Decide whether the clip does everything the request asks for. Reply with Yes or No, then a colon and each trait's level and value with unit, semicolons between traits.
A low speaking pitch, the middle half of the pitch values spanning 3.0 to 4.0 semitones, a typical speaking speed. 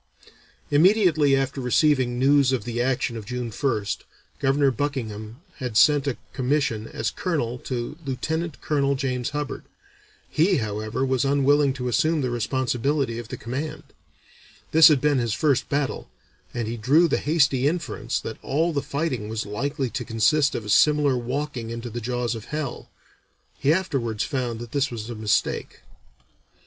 Yes: low, 130 Hz; average, 3.6 semitones; average, 160 wpm